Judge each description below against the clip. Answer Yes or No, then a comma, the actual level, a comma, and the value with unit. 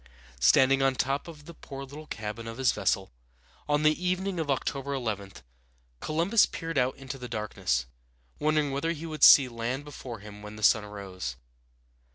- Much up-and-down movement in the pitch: Yes, wide, 6.0 semitones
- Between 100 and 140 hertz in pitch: Yes, low, 135 Hz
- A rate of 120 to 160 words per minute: No, average, 175 wpm